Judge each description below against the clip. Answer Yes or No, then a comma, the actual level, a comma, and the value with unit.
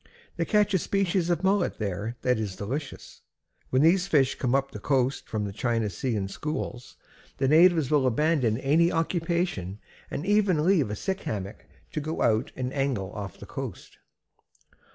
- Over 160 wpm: Yes, average, 175 wpm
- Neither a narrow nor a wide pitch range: No, wide, 7.4 semitones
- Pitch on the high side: No, low, 135 Hz